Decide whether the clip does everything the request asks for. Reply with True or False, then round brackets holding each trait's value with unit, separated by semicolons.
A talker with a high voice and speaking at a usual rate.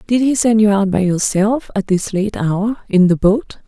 False (205 Hz; 230 wpm)